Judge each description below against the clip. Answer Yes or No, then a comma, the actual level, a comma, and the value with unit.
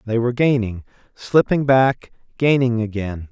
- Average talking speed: No, slow, 90 wpm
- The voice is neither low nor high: No, low, 120 Hz